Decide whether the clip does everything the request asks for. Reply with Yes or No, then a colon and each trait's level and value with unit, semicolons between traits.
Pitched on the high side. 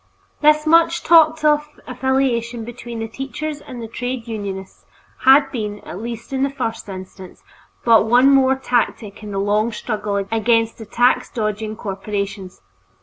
Yes: high, 235 Hz